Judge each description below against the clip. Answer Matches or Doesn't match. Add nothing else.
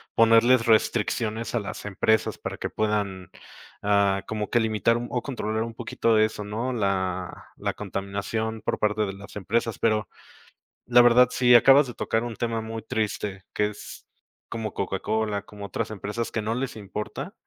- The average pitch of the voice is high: Doesn't match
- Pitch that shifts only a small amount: Matches